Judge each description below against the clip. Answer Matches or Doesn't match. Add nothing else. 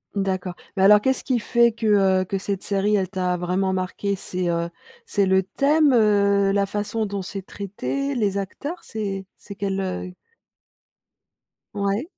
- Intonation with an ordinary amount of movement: Doesn't match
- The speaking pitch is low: Doesn't match